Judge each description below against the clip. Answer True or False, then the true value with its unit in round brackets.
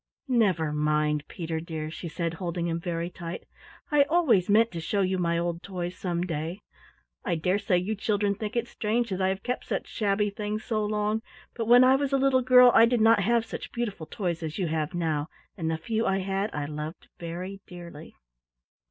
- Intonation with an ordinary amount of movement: True (4.5 semitones)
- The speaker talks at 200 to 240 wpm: True (205 wpm)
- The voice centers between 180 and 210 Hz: True (185 Hz)